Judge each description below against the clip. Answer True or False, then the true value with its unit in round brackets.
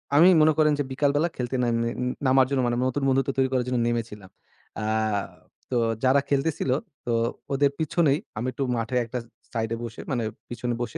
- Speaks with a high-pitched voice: False (130 Hz)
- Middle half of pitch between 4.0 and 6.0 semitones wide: False (2.9 semitones)